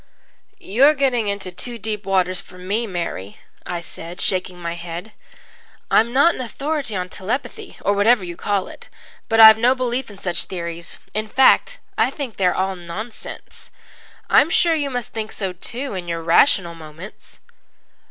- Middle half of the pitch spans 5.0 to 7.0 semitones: Yes, average, 5.3 semitones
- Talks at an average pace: Yes, average, 170 wpm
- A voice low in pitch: No, high, 200 Hz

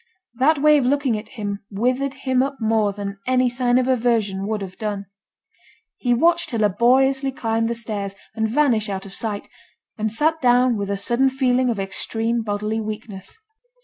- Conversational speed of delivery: Yes, average, 180 wpm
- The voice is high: Yes, high, 230 Hz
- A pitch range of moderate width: Yes, average, 3.7 semitones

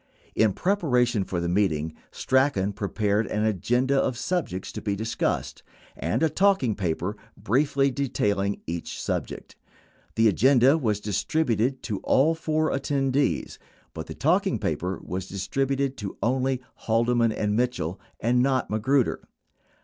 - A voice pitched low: Yes, low, 120 Hz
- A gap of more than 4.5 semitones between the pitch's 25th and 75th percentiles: Yes, average, 5.2 semitones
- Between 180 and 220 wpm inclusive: No, average, 140 wpm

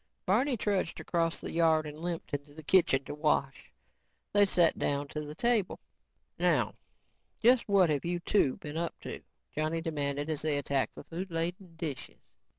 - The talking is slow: No, average, 170 wpm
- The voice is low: No, medium, 165 Hz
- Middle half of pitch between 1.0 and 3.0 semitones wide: No, average, 3.6 semitones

